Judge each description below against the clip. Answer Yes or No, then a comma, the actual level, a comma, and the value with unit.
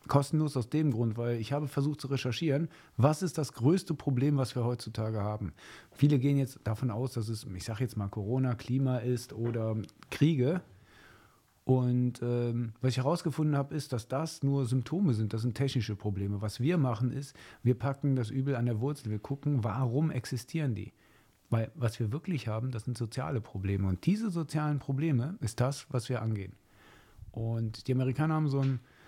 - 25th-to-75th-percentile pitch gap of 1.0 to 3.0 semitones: No, average, 3.8 semitones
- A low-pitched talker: Yes, low, 125 Hz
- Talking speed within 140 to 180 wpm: No, fast, 190 wpm